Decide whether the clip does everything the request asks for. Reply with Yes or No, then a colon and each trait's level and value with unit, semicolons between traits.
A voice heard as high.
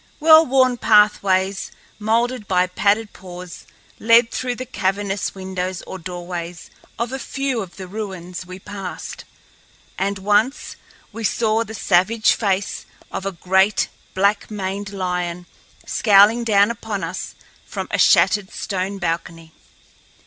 Yes: high, 200 Hz